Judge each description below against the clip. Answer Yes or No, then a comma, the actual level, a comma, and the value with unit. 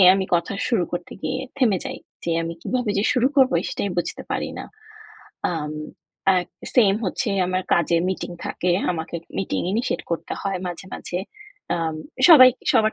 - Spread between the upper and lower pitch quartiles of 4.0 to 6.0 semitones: Yes, average, 5.1 semitones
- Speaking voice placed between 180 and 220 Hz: Yes, high, 190 Hz